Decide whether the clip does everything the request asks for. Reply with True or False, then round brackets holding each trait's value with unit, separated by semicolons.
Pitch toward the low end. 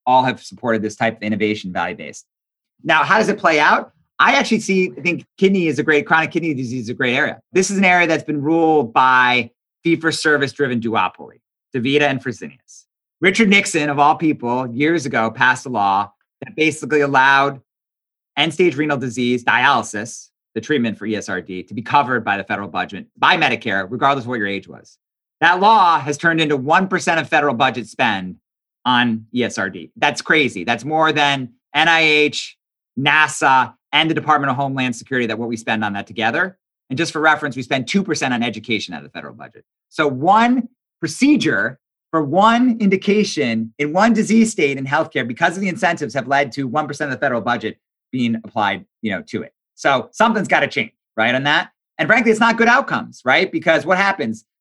False (145 Hz)